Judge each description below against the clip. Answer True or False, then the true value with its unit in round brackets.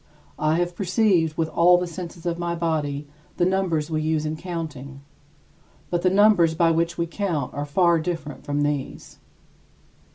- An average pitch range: False (2.3 semitones)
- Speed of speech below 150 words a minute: False (165 wpm)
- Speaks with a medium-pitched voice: True (165 Hz)